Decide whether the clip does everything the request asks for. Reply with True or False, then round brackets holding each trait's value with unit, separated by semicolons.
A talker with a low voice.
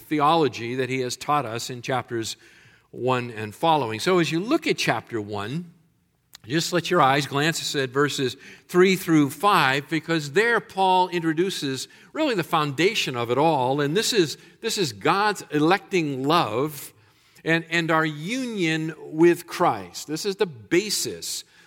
False (160 Hz)